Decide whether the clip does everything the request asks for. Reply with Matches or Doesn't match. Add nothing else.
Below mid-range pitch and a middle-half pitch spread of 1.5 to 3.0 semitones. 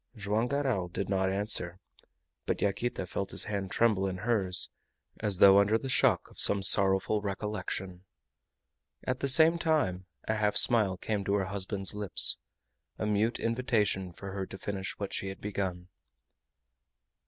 Matches